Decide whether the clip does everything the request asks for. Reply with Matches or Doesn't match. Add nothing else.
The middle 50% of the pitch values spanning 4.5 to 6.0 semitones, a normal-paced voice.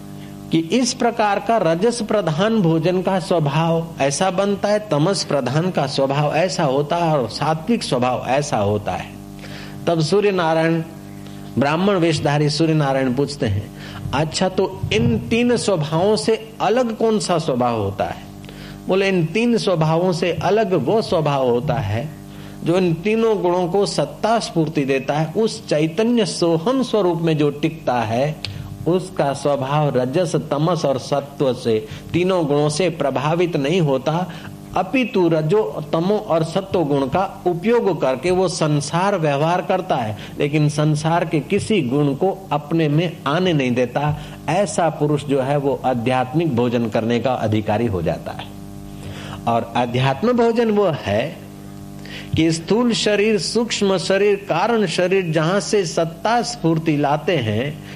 Matches